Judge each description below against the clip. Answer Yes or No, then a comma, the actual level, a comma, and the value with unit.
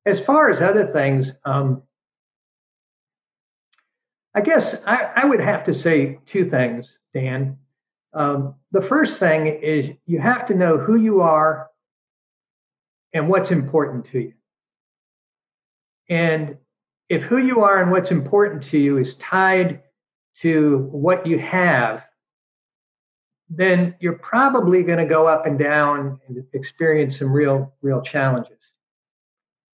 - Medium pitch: Yes, medium, 155 Hz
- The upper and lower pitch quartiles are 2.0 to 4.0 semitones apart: No, average, 4.8 semitones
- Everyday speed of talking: No, slow, 130 wpm